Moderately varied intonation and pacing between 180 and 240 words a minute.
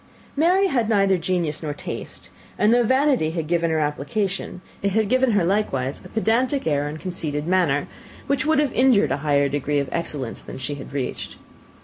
No: wide, 7.5 semitones; average, 190 wpm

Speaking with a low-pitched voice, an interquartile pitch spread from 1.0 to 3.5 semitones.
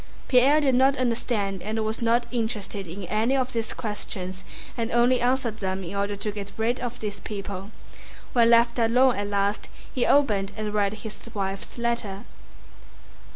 No: high, 220 Hz; average, 3.2 semitones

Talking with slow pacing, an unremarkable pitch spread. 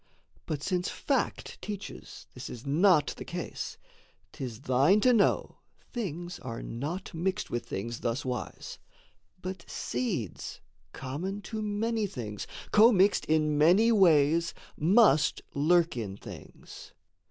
No: slow, 120 wpm; wide, 6.7 semitones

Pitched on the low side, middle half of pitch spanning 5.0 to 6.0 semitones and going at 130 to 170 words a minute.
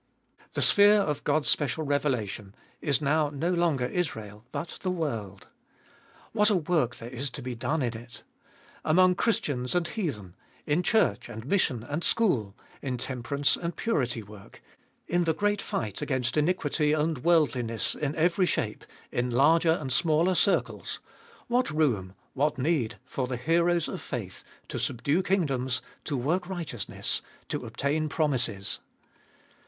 No: medium, 145 Hz; wide, 5.6 semitones; average, 150 wpm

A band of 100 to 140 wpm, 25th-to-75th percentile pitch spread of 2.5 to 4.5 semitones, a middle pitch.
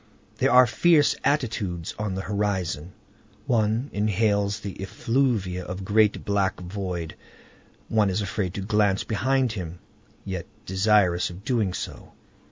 No: slow, 135 wpm; average, 2.9 semitones; low, 100 Hz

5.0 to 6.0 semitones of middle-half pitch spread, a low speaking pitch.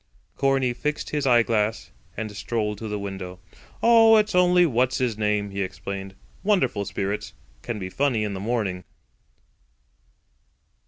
Yes: wide, 5.4 semitones; low, 110 Hz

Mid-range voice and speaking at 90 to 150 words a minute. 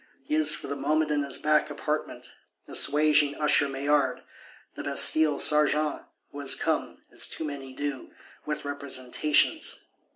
Yes: medium, 145 Hz; average, 140 wpm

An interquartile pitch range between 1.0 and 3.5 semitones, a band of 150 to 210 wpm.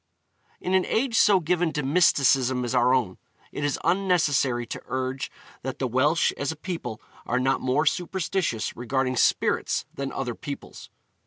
No: average, 5.1 semitones; average, 160 wpm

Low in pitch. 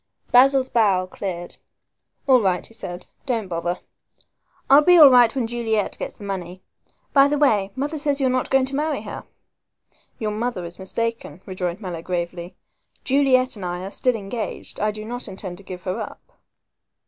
No: high, 215 Hz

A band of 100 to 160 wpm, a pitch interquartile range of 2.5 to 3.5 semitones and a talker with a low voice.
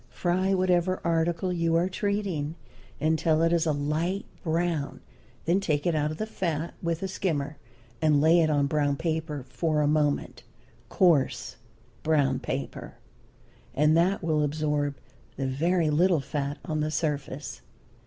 No: average, 150 wpm; average, 2.8 semitones; medium, 160 Hz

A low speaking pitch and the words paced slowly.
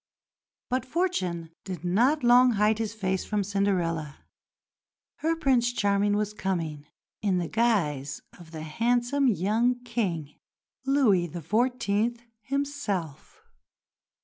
No: high, 210 Hz; slow, 110 wpm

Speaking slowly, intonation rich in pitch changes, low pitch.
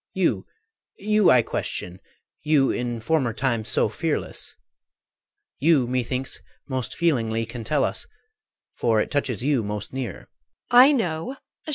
No: slow, 115 wpm; average, 3.9 semitones; low, 125 Hz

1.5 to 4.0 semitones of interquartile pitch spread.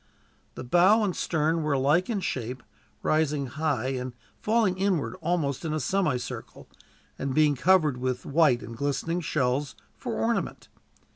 No: average, 5.2 semitones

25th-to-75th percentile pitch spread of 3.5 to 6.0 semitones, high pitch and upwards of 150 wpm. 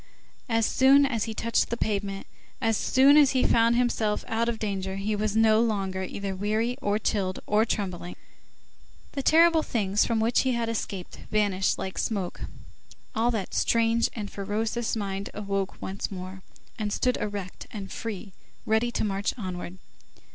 No: average, 2.9 semitones; high, 215 Hz; average, 160 wpm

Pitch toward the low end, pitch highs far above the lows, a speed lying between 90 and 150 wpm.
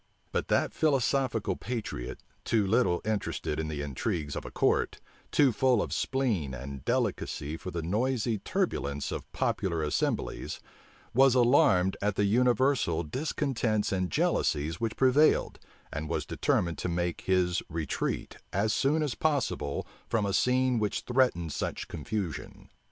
Yes: low, 105 Hz; wide, 7.2 semitones; average, 140 wpm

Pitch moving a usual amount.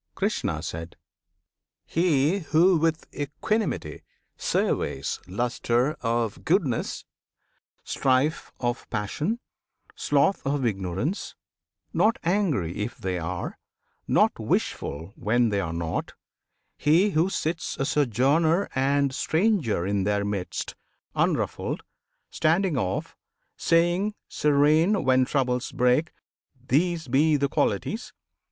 No: wide, 7.2 semitones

